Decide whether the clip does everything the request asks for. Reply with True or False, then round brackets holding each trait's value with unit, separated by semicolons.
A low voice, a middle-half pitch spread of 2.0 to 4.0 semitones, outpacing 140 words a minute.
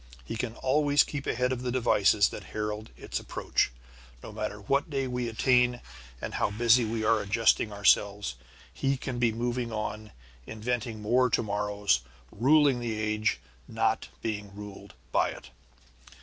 True (115 Hz; 3.0 semitones; 155 wpm)